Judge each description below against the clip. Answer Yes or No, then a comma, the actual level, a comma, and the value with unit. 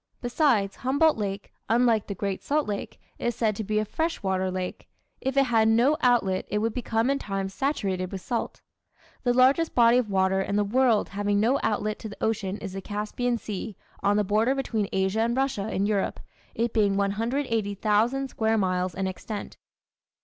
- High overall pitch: Yes, high, 215 Hz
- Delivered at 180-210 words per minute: Yes, average, 185 wpm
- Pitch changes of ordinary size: Yes, average, 3.5 semitones